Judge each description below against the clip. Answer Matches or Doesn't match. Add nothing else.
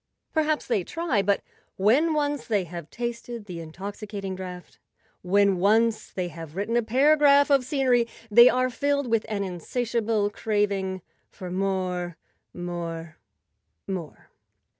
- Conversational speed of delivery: Doesn't match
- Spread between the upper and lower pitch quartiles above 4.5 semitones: Matches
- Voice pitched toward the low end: Doesn't match